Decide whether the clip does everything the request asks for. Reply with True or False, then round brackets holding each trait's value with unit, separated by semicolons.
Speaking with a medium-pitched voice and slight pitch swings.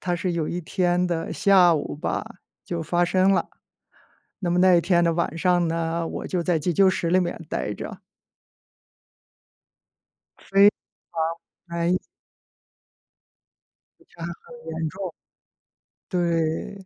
True (175 Hz; 1.7 semitones)